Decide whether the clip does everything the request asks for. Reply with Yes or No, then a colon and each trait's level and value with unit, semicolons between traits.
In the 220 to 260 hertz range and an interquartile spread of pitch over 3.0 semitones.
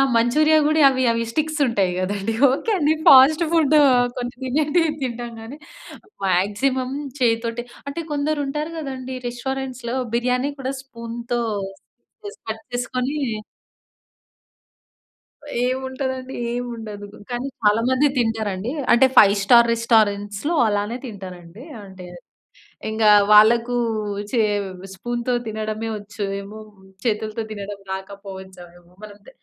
Yes: high, 235 Hz; average, 3.9 semitones